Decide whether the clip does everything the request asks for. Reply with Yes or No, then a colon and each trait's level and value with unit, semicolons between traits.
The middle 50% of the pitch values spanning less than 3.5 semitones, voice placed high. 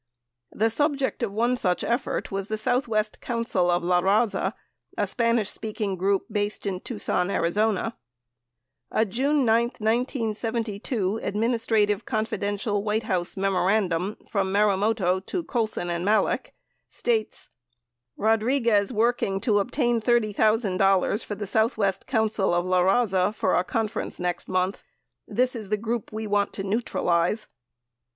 Yes: average, 2.9 semitones; high, 215 Hz